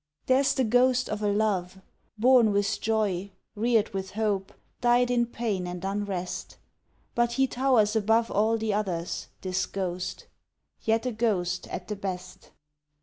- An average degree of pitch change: Yes, average, 3.6 semitones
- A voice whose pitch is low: No, high, 210 Hz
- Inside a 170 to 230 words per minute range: No, average, 145 wpm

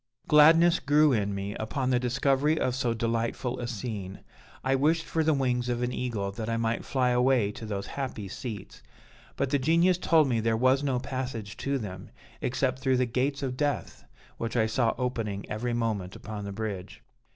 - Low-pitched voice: Yes, low, 125 Hz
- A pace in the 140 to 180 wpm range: No, average, 190 wpm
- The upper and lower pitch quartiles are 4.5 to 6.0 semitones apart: No, average, 3.5 semitones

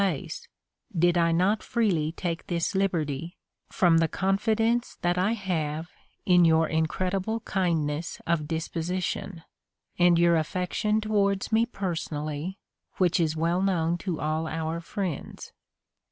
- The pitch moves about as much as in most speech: Yes, average, 3.2 semitones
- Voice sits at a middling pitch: Yes, medium, 175 Hz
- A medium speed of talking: No, slow, 125 wpm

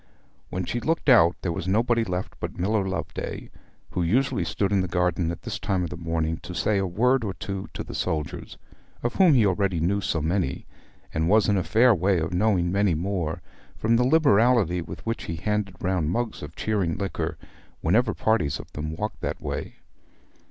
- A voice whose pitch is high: No, very low, 95 Hz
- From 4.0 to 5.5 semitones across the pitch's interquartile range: Yes, average, 4.3 semitones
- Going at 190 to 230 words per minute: Yes, average, 200 wpm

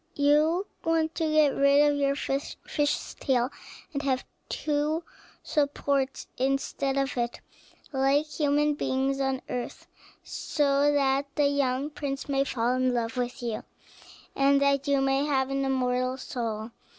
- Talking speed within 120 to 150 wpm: Yes, average, 145 wpm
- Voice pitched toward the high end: Yes, very high, 275 Hz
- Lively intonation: No, narrow, 1.8 semitones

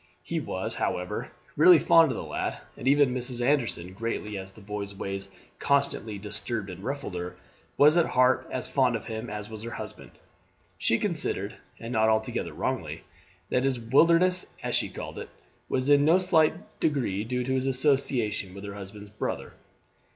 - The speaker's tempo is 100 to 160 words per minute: No, average, 175 wpm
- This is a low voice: Yes, low, 120 Hz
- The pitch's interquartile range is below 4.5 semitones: No, average, 5.2 semitones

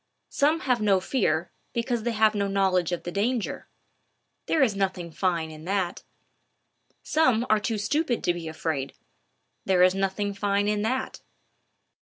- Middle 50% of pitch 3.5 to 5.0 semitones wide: Yes, average, 4.2 semitones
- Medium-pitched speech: No, high, 200 Hz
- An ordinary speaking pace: Yes, average, 155 wpm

